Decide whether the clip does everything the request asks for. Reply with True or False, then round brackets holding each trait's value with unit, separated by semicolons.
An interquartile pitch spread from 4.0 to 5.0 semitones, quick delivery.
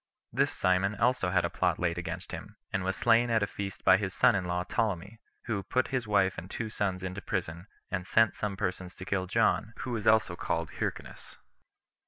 False (3.1 semitones; 210 wpm)